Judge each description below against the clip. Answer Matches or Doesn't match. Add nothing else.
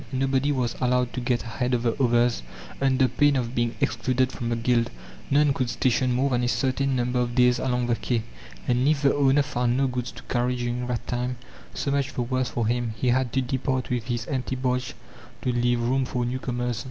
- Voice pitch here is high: Doesn't match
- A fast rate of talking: Matches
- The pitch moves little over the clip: Matches